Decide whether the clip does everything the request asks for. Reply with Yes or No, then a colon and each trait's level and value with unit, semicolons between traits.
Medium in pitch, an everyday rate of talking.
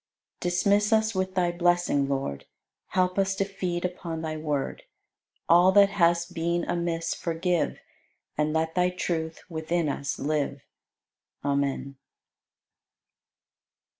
No: medium, 170 Hz; slow, 120 wpm